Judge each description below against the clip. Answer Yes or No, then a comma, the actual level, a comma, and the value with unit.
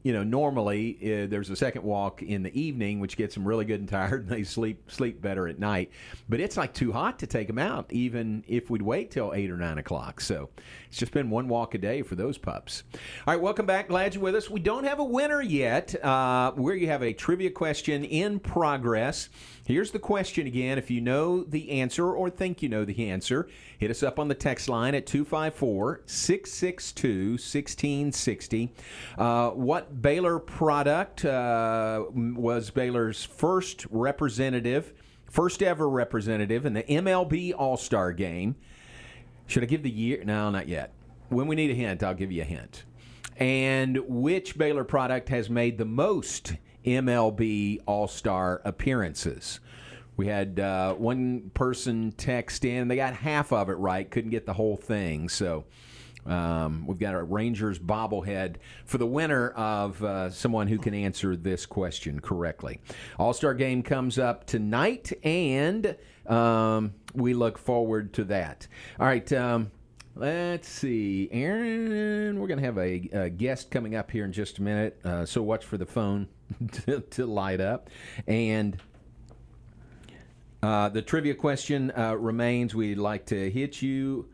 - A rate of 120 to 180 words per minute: Yes, average, 170 wpm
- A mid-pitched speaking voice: No, low, 120 Hz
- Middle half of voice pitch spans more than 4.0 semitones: Yes, average, 4.9 semitones